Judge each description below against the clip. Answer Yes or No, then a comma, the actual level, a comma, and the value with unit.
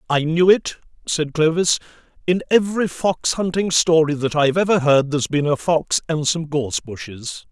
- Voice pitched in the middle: Yes, medium, 160 Hz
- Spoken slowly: No, average, 175 wpm